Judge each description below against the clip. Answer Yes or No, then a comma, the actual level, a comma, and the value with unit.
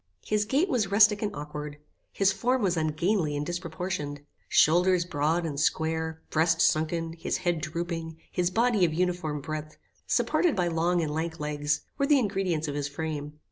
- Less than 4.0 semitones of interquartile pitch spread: Yes, average, 3.5 semitones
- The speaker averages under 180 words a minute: Yes, average, 170 wpm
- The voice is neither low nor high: Yes, medium, 165 Hz